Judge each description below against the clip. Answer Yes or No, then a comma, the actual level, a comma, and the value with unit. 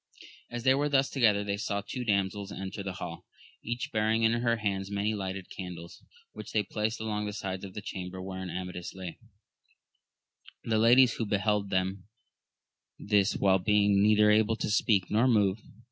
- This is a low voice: Yes, low, 105 Hz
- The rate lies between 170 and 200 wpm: Yes, average, 175 wpm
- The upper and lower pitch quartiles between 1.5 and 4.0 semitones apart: Yes, narrow, 2.4 semitones